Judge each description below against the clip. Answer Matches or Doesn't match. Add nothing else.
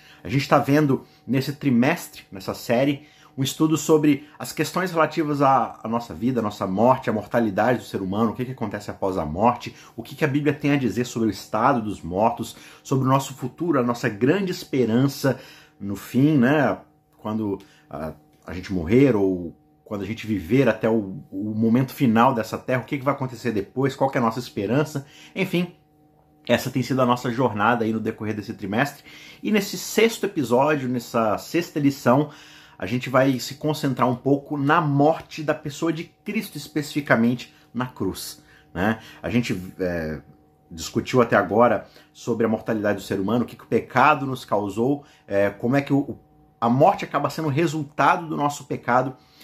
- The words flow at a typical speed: Doesn't match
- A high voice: Doesn't match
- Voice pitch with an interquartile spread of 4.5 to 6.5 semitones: Matches